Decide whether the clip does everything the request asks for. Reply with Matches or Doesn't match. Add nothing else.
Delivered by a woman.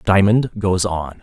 Doesn't match